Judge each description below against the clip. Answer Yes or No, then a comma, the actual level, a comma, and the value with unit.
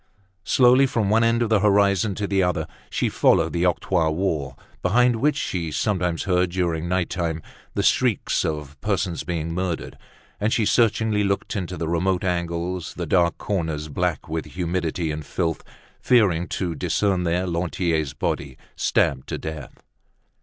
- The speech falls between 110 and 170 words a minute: Yes, average, 160 wpm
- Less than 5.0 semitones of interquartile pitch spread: Yes, average, 3.3 semitones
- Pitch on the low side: Yes, very low, 90 Hz